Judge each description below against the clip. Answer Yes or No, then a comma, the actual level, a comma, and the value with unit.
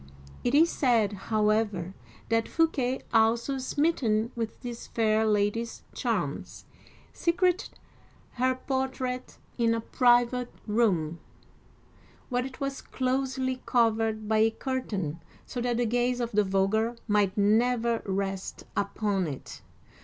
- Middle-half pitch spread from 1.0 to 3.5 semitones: Yes, average, 3.2 semitones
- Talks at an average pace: No, slow, 120 wpm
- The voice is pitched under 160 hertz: No, high, 230 Hz